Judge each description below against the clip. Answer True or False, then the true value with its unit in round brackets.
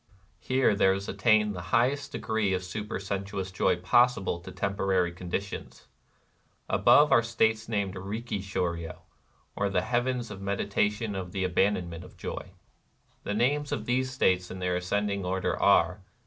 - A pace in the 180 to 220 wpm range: False (160 wpm)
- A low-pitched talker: True (100 Hz)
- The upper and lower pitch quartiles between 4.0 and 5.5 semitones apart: False (3.2 semitones)